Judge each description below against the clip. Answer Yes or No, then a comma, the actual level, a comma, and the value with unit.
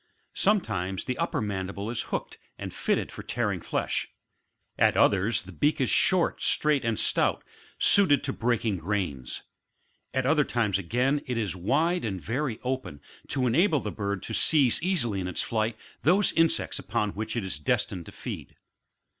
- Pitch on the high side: No, low, 115 Hz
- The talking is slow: No, average, 165 wpm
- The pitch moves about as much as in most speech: No, wide, 6.4 semitones